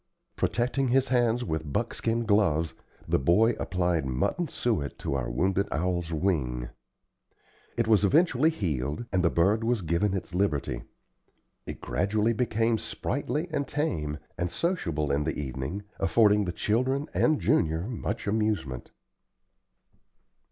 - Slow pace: Yes, slow, 130 wpm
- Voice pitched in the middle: No, low, 100 Hz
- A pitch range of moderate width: No, wide, 6.8 semitones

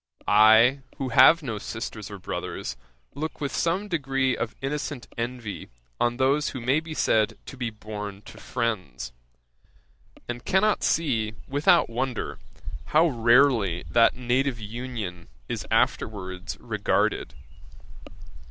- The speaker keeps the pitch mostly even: No, average, 4.3 semitones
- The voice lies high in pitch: No, low, 120 Hz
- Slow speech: Yes, slow, 125 wpm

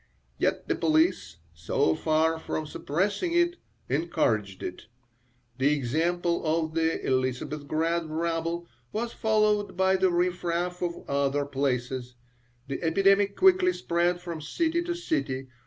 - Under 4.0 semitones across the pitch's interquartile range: No, average, 4.9 semitones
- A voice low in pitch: No, medium, 165 Hz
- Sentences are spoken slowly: Yes, slow, 125 wpm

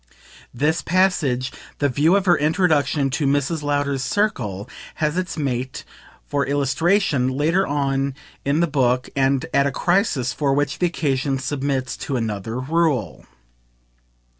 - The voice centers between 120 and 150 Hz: Yes, medium, 140 Hz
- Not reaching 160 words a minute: Yes, average, 140 wpm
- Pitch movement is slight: No, average, 3.5 semitones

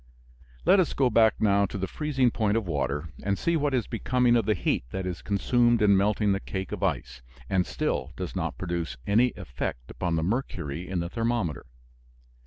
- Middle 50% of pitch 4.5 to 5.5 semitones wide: Yes, average, 5.1 semitones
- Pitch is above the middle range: No, low, 100 Hz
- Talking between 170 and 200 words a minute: Yes, average, 195 wpm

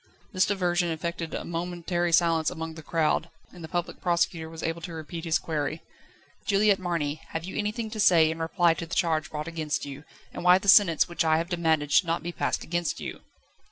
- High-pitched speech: No, medium, 170 Hz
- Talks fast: Yes, fast, 210 wpm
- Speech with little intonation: Yes, narrow, 1.7 semitones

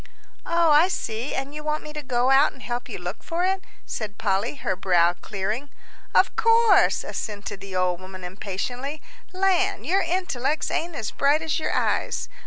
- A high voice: Yes, very high, 270 Hz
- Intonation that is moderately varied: No, wide, 8.5 semitones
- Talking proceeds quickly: No, average, 180 wpm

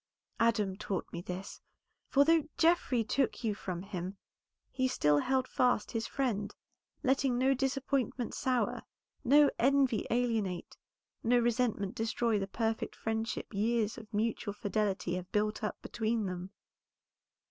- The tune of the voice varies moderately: Yes, average, 4.0 semitones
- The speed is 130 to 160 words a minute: Yes, slow, 135 wpm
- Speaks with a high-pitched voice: Yes, high, 225 Hz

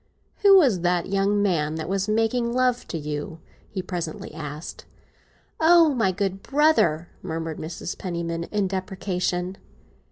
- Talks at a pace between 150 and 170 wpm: No, slow, 135 wpm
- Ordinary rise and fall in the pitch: Yes, average, 4.7 semitones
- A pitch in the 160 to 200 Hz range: Yes, medium, 185 Hz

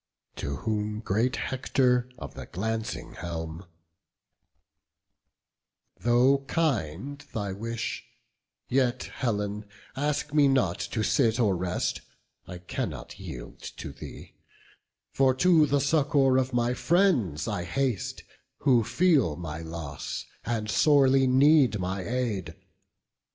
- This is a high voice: No, low, 120 Hz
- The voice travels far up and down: Yes, wide, 5.9 semitones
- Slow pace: Yes, slow, 115 wpm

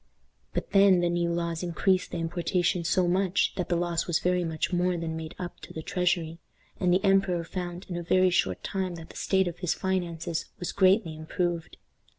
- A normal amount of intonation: No, narrow, 1.7 semitones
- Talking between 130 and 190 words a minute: No, average, 200 wpm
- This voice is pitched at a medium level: Yes, medium, 175 Hz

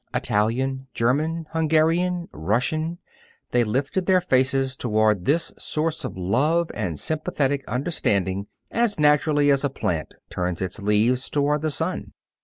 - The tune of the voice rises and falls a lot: Yes, wide, 6.6 semitones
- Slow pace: Yes, slow, 130 wpm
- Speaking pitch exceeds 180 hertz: No, low, 135 Hz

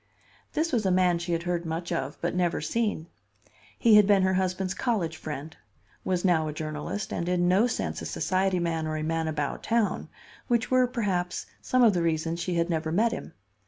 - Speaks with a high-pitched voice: No, medium, 175 Hz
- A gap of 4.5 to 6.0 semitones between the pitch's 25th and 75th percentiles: No, average, 3.7 semitones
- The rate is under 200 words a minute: No, fast, 205 wpm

